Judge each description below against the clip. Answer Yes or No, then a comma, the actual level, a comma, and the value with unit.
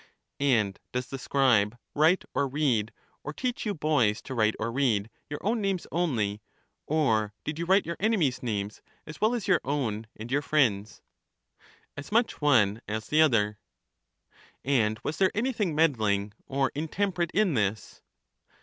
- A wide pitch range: Yes, wide, 7.0 semitones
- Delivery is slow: No, average, 160 wpm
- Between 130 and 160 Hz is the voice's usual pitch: Yes, medium, 140 Hz